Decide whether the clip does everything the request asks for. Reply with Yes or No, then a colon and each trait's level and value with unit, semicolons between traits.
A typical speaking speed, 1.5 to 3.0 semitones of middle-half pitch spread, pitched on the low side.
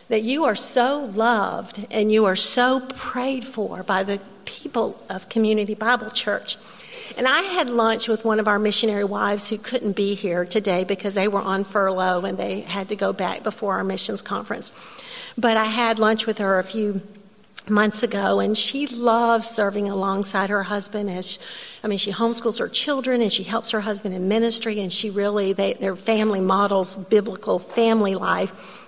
No: average, 185 wpm; narrow, 2.5 semitones; high, 210 Hz